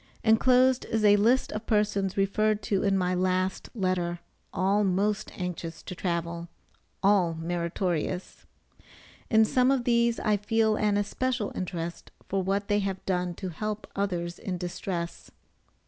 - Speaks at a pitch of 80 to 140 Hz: No, high, 195 Hz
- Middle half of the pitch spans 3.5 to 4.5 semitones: No, average, 3.0 semitones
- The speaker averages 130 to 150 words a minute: Yes, average, 145 wpm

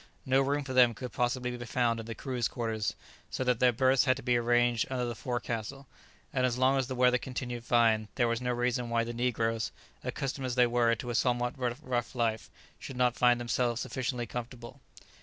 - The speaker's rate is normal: No, fast, 210 wpm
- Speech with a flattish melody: Yes, narrow, 1.4 semitones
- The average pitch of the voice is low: Yes, low, 120 Hz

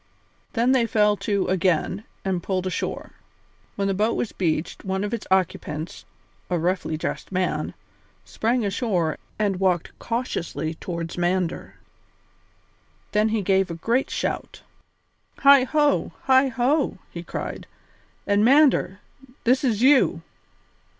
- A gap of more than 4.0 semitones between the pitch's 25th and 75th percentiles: Yes, average, 4.9 semitones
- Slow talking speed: Yes, slow, 125 wpm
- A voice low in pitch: No, high, 200 Hz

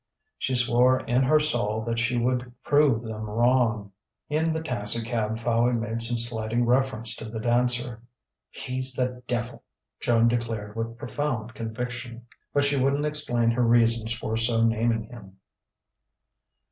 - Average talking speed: Yes, average, 145 wpm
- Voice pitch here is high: No, low, 120 Hz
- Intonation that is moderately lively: No, narrow, 1.7 semitones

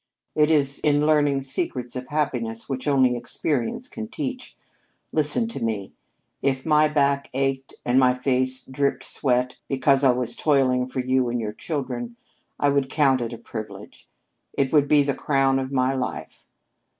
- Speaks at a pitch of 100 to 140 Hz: Yes, low, 135 Hz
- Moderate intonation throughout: No, narrow, 2.3 semitones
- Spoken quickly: No, average, 165 wpm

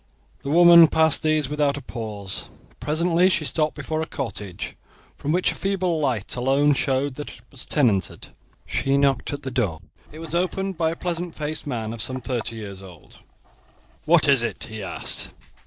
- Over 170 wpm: Yes, average, 180 wpm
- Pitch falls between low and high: Yes, medium, 145 Hz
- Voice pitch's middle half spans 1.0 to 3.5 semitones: No, average, 5.2 semitones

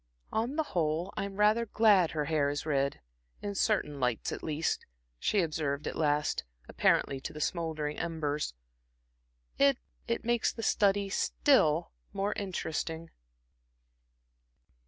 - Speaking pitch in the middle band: Yes, medium, 165 Hz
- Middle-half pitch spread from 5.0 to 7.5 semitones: Yes, wide, 5.5 semitones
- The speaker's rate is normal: No, slow, 130 wpm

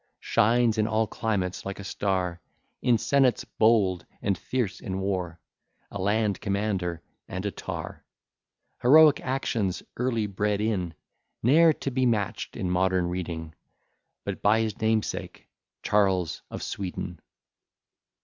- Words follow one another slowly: Yes, slow, 130 wpm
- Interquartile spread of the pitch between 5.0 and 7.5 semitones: No, average, 3.4 semitones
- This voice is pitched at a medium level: No, low, 100 Hz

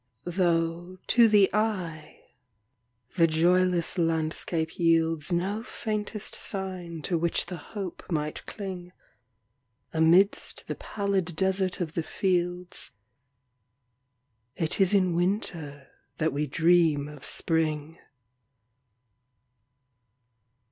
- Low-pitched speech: No, medium, 170 Hz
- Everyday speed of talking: No, slow, 85 wpm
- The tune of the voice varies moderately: Yes, average, 3.6 semitones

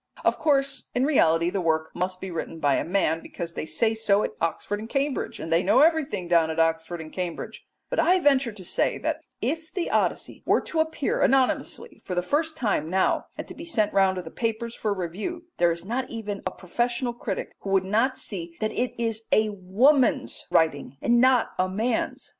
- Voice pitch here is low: No, high, 210 Hz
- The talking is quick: Yes, fast, 210 wpm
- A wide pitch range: Yes, wide, 6.8 semitones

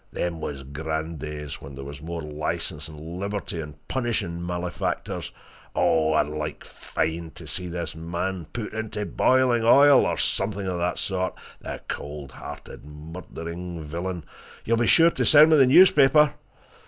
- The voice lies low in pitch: Yes, very low, 85 Hz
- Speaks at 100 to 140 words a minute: No, average, 155 wpm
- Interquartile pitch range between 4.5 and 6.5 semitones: Yes, average, 5.2 semitones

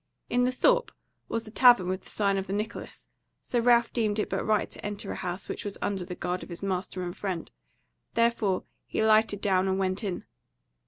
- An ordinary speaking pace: No, fast, 215 wpm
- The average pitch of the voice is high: Yes, high, 205 Hz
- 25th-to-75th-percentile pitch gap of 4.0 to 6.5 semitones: No, average, 3.3 semitones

